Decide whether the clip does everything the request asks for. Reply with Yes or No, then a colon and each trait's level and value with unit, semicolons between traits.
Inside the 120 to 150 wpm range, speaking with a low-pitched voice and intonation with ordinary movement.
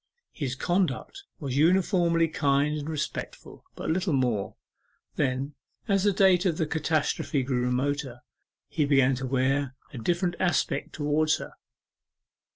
No: slow, 135 wpm; medium, 150 Hz; average, 4.3 semitones